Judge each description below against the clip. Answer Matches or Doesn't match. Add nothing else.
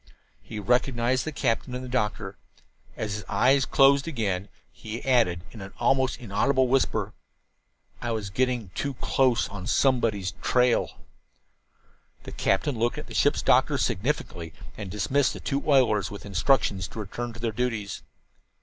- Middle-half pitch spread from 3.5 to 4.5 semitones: Matches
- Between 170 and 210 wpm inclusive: Doesn't match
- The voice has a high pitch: Doesn't match